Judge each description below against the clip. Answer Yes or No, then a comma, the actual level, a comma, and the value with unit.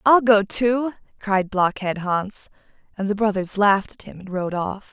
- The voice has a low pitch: No, high, 205 Hz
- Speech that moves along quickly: No, average, 185 wpm